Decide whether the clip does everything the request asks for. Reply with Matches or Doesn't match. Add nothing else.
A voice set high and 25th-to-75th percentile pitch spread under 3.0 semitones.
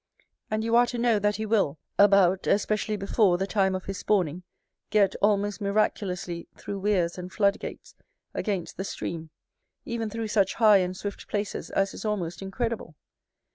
Matches